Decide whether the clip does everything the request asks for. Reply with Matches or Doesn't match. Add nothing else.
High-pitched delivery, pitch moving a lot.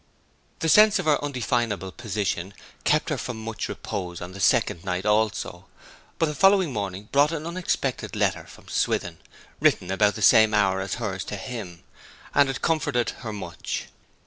Doesn't match